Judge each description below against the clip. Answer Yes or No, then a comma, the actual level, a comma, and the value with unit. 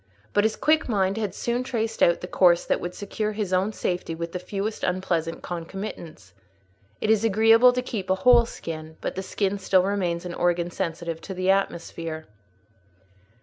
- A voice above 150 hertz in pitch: Yes, high, 190 Hz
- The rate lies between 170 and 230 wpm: Yes, average, 180 wpm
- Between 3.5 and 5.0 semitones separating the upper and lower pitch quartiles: Yes, average, 3.9 semitones